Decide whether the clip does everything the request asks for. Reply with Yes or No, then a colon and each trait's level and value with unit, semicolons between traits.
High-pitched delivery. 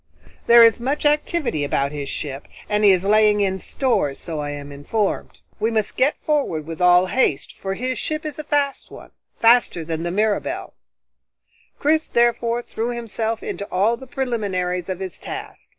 Yes: high, 210 Hz